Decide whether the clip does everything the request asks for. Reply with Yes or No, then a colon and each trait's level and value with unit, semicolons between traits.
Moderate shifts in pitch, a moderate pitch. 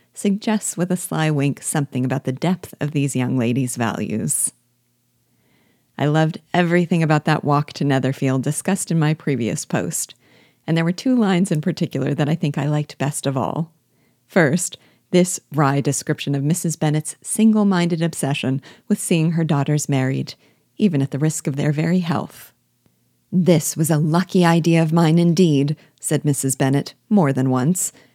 Yes: average, 4.0 semitones; medium, 155 Hz